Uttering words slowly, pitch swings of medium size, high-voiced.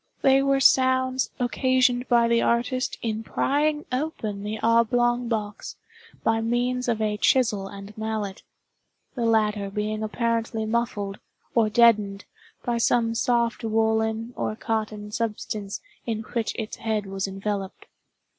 No: slow, 125 wpm; narrow, 2.3 semitones; high, 225 Hz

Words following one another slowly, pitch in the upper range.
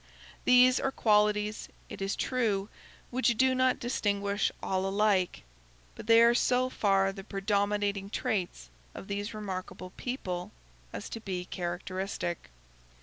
Yes: slow, 130 wpm; high, 205 Hz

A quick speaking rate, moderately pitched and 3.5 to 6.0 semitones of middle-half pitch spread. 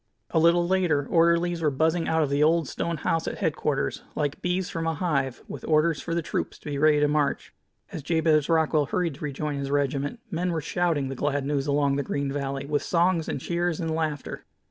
No: fast, 215 wpm; medium, 155 Hz; average, 2.8 semitones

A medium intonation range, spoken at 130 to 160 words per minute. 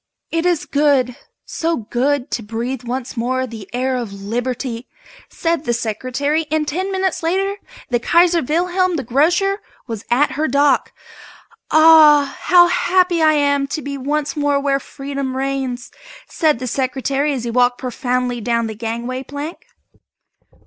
Yes: average, 4.2 semitones; average, 150 wpm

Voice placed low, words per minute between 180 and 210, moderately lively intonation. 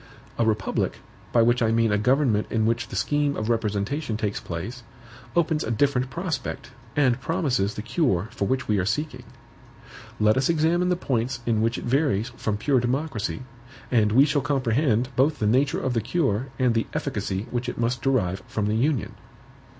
Yes: low, 120 Hz; average, 185 wpm; average, 4.4 semitones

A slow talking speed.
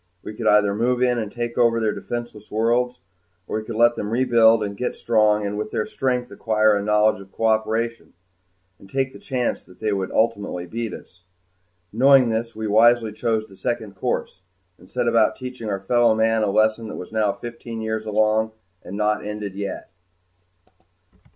No: average, 185 wpm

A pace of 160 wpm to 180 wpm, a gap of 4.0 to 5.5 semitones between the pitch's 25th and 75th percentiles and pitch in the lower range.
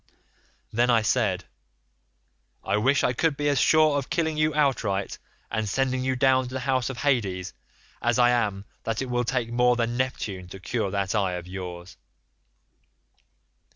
Yes: average, 170 wpm; average, 4.8 semitones; low, 120 Hz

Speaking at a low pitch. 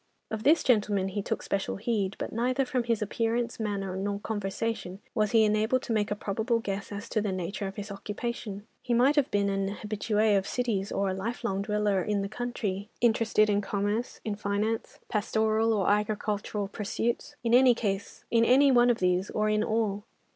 No: high, 210 Hz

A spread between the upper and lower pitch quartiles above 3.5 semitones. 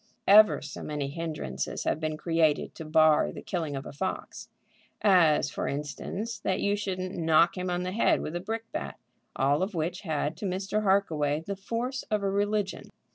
Yes: average, 4.4 semitones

